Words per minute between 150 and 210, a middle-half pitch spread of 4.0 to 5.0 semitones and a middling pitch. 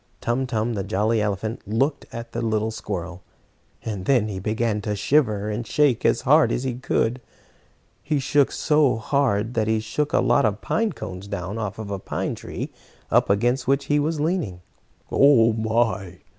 No: average, 175 wpm; average, 4.3 semitones; low, 110 Hz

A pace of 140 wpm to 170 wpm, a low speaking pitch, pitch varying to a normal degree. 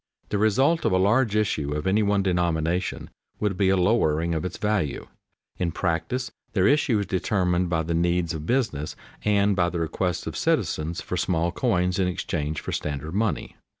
No: average, 185 wpm; very low, 90 Hz; average, 3.7 semitones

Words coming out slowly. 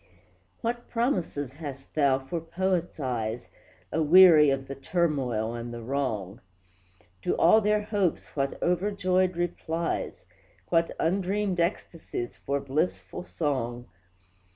Yes: slow, 110 wpm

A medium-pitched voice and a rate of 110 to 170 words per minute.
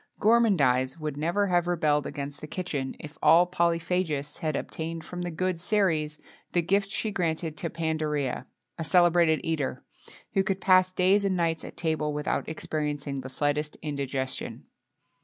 Yes: medium, 160 Hz; average, 155 wpm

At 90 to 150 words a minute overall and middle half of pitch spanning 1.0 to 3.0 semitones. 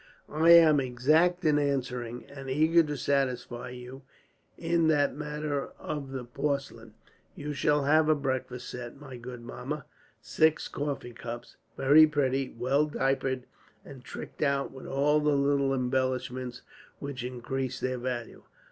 Yes: average, 140 wpm; narrow, 2.6 semitones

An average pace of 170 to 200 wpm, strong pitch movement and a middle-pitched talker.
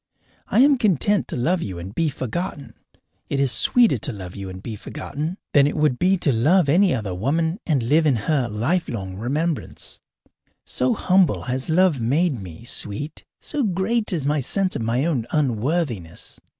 Yes: average, 175 wpm; wide, 7.0 semitones; medium, 145 Hz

